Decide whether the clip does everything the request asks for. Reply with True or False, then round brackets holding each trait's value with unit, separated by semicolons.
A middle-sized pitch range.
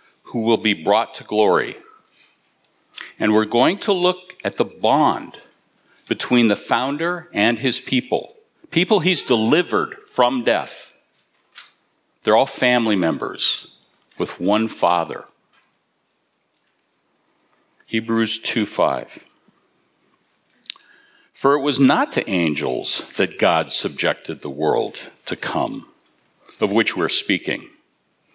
False (7.3 semitones)